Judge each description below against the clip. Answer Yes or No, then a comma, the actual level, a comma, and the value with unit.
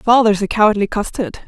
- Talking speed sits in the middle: Yes, average, 165 wpm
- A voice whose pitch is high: Yes, high, 215 Hz